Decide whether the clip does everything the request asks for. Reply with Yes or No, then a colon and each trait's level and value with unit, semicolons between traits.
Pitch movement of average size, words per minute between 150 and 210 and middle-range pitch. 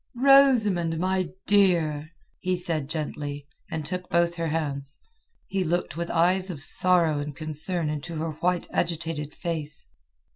No: average, 3.0 semitones; average, 140 wpm; medium, 165 Hz